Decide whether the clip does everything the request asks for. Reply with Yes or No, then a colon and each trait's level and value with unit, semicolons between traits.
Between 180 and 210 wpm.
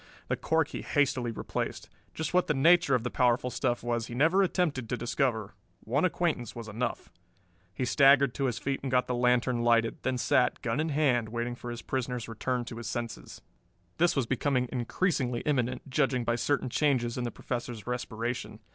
Yes: average, 190 wpm